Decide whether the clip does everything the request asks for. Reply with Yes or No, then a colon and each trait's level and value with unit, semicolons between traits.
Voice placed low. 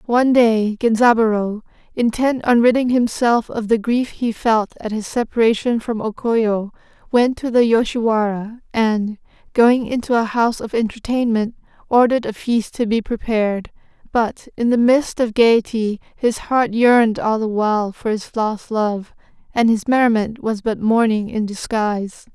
No: high, 225 Hz